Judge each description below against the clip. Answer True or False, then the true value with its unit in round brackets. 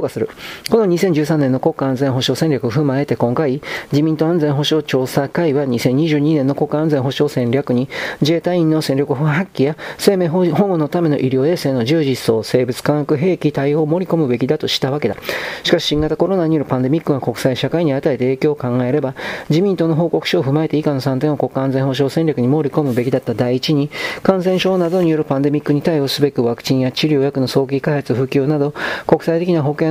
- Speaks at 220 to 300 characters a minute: False (410 characters per minute)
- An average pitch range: True (3.2 semitones)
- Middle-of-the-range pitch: True (150 Hz)